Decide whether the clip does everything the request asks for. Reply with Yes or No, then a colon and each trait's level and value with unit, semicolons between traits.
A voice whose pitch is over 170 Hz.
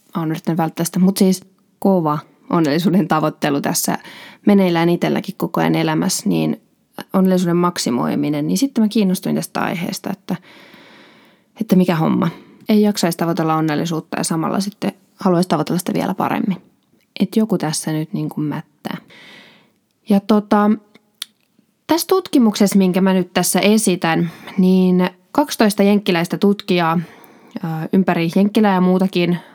Yes: medium, 185 Hz